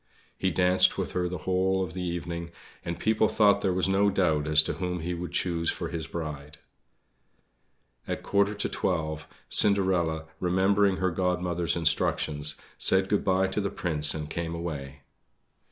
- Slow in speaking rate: No, average, 170 wpm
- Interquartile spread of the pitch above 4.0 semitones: No, average, 2.8 semitones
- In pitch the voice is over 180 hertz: No, very low, 90 Hz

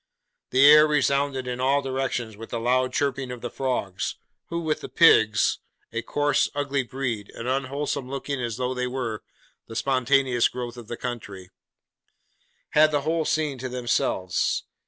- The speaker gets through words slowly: No, average, 160 wpm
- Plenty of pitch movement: No, average, 2.7 semitones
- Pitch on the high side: No, low, 130 Hz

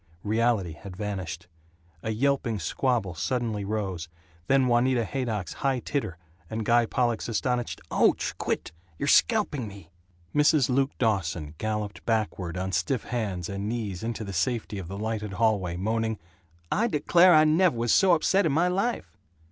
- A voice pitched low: Yes, low, 110 Hz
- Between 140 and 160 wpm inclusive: Yes, average, 155 wpm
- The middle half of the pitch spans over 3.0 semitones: Yes, average, 5.0 semitones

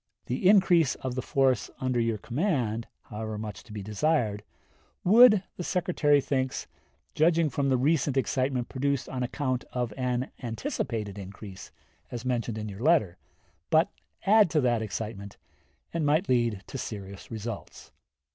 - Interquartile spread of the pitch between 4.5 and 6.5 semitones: Yes, average, 5.2 semitones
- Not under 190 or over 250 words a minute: No, average, 145 wpm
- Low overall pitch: Yes, low, 125 Hz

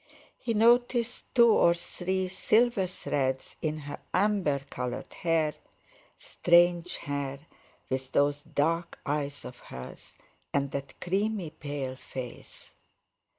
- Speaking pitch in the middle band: Yes, medium, 160 Hz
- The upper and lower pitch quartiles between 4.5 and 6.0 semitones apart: Yes, average, 5.1 semitones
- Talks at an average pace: No, slow, 110 wpm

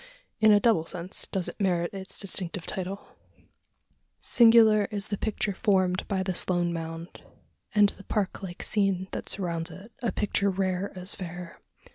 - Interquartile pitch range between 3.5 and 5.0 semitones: No, narrow, 2.4 semitones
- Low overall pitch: No, high, 190 Hz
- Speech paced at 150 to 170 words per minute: Yes, average, 160 wpm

